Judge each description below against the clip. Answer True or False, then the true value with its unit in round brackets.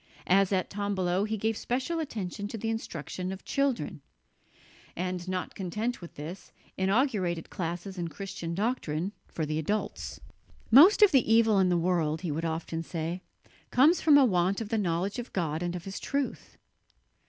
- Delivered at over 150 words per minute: True (170 wpm)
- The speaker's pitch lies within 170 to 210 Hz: True (190 Hz)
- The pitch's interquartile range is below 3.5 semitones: False (4.6 semitones)